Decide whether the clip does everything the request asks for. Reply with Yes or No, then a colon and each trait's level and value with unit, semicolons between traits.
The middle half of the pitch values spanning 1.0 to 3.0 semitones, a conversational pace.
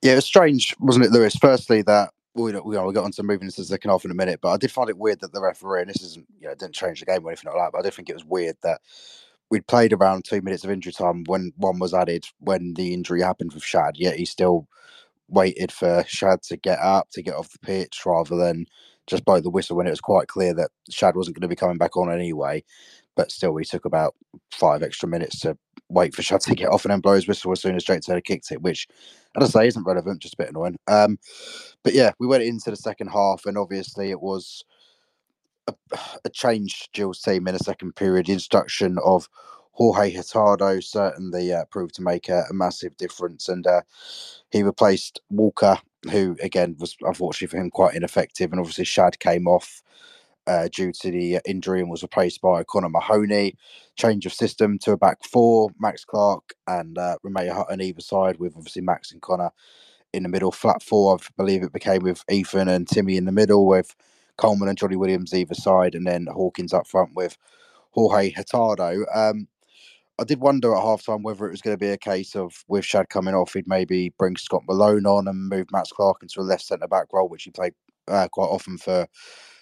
No: narrow, 2.4 semitones; fast, 230 wpm